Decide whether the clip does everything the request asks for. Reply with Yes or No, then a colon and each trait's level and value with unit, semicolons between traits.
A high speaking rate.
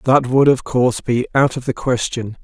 Yes: fast, 220 wpm